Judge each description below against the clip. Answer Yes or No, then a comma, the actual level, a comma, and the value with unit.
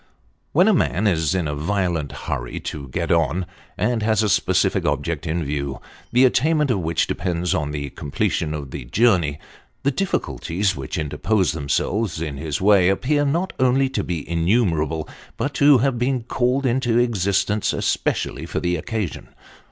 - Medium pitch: No, very low, 95 Hz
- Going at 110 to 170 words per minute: Yes, average, 165 wpm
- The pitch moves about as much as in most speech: No, wide, 7.7 semitones